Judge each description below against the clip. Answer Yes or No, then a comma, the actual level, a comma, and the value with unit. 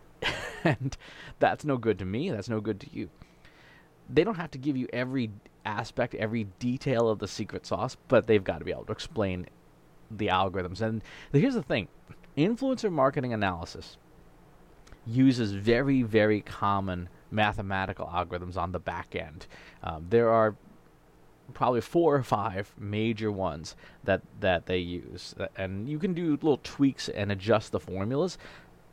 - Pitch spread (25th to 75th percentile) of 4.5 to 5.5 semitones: Yes, average, 5.0 semitones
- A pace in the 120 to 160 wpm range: Yes, average, 155 wpm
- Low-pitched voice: Yes, low, 110 Hz